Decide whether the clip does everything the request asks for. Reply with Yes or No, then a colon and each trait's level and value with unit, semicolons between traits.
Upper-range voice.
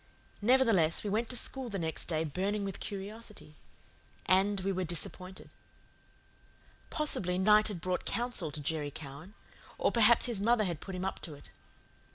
Yes: high, 195 Hz